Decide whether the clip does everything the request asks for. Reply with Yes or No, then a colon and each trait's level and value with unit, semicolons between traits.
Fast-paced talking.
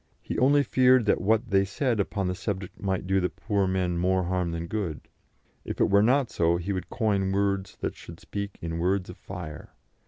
Yes: fast, 210 wpm